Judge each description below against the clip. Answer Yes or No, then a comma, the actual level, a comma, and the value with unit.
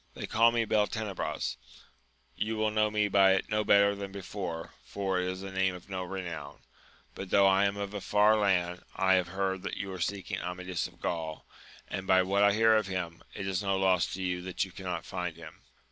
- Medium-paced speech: No, fast, 225 wpm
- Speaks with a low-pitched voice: Yes, very low, 95 Hz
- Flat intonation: Yes, narrow, 1.8 semitones